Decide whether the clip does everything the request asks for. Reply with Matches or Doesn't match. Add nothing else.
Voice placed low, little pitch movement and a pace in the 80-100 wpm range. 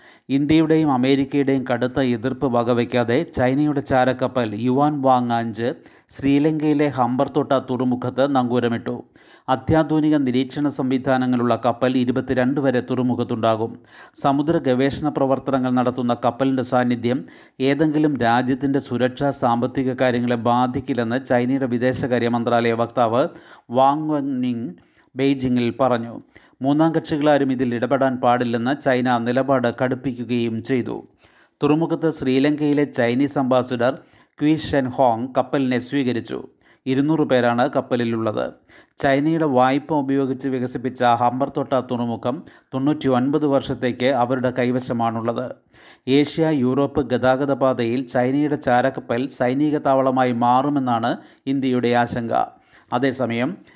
Matches